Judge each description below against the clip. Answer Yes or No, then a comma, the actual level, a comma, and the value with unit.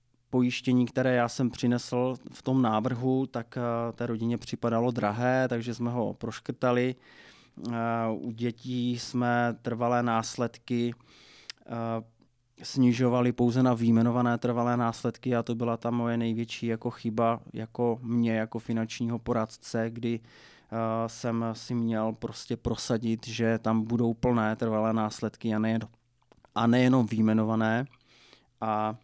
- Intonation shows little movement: Yes, narrow, 1.2 semitones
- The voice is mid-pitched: No, low, 120 Hz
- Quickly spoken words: No, average, 130 wpm